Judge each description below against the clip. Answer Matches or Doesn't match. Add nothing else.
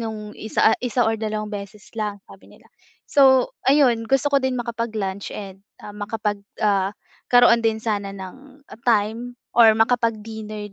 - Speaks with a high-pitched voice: Matches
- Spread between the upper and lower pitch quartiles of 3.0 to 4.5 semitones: Doesn't match